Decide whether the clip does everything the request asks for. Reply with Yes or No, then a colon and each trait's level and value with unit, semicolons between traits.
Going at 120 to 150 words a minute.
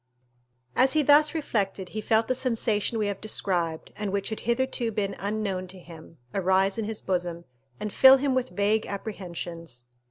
No: average, 170 wpm